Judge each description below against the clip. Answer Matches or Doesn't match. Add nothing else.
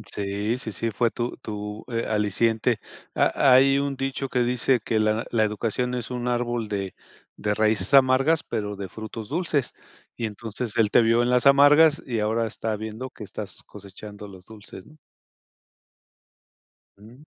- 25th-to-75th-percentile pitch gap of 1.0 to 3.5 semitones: Matches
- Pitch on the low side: Matches